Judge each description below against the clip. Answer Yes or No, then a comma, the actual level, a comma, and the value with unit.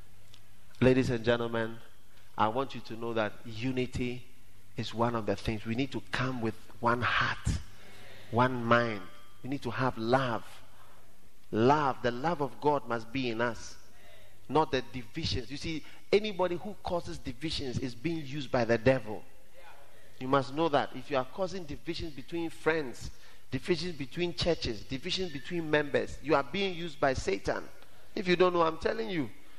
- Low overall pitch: Yes, low, 125 Hz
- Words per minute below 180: Yes, average, 170 wpm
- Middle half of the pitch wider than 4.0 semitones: Yes, average, 4.4 semitones